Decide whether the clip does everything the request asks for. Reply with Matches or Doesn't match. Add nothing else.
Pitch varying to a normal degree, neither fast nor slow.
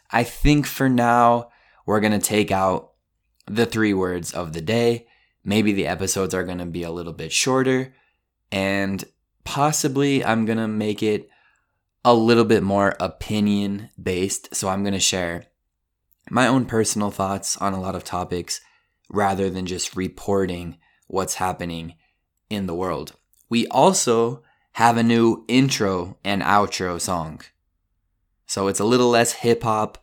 Matches